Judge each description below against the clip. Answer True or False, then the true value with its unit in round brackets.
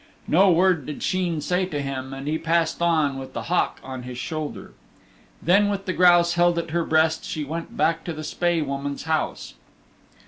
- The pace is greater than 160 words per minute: True (195 wpm)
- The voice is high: False (160 Hz)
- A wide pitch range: False (3.1 semitones)